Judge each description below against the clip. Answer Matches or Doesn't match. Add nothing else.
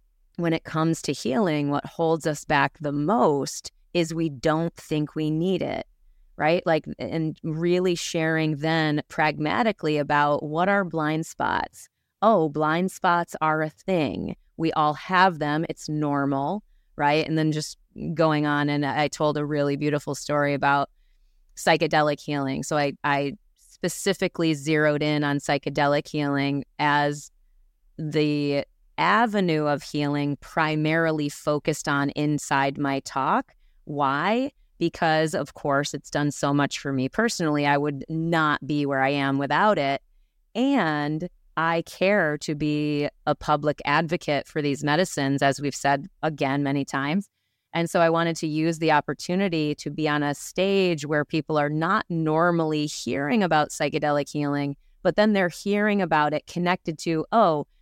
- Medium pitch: Matches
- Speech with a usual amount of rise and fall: Doesn't match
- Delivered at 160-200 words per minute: Doesn't match